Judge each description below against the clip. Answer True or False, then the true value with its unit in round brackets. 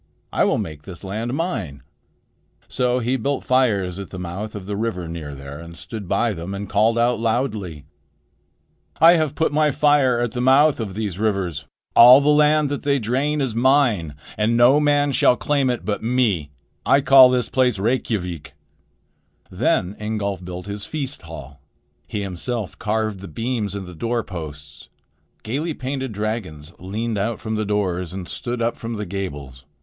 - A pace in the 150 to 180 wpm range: True (175 wpm)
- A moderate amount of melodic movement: False (5.7 semitones)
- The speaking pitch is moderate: False (110 Hz)